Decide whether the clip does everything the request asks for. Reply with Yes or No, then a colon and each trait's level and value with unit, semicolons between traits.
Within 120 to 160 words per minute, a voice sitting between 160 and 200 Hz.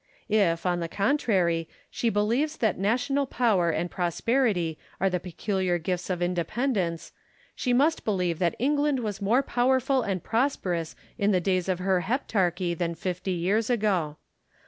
Yes: average, 150 wpm; high, 190 Hz